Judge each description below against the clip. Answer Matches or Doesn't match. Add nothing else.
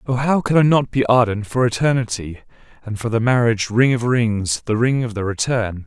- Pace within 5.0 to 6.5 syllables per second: Matches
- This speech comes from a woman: Doesn't match